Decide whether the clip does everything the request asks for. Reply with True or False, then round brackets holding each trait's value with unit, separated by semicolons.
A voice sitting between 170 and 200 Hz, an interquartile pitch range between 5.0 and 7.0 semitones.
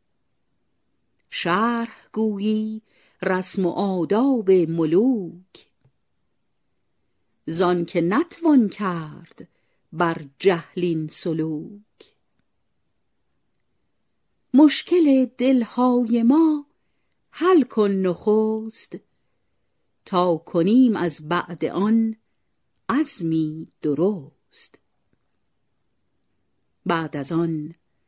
True (190 Hz; 5.6 semitones)